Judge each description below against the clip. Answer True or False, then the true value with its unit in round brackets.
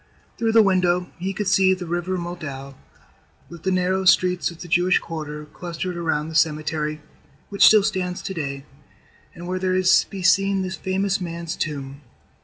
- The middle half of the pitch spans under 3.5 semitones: True (2.8 semitones)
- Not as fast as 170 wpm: False (175 wpm)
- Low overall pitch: False (180 Hz)